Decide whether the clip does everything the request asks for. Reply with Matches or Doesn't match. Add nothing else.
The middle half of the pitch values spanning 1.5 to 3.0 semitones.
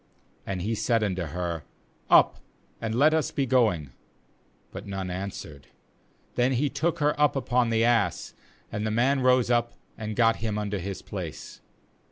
Doesn't match